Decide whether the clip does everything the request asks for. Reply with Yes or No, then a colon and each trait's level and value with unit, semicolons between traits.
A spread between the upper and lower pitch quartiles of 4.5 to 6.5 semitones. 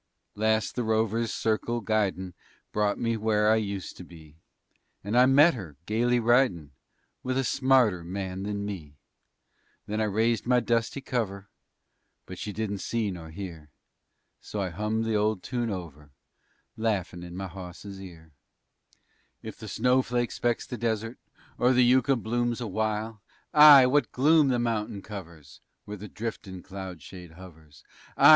No: average, 4.1 semitones